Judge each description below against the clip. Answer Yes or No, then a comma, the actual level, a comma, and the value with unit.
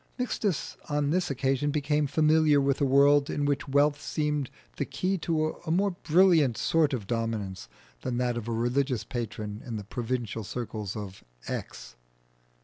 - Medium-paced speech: Yes, average, 160 wpm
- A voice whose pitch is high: No, medium, 140 Hz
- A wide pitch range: No, average, 4.6 semitones